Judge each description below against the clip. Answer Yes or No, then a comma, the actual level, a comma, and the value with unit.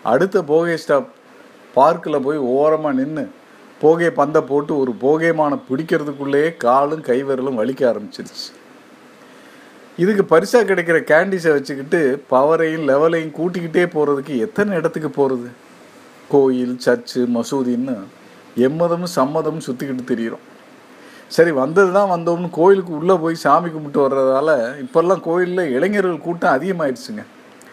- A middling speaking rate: Yes, average, 110 wpm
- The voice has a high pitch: No, medium, 155 Hz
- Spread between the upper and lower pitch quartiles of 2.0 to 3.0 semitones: No, average, 4.1 semitones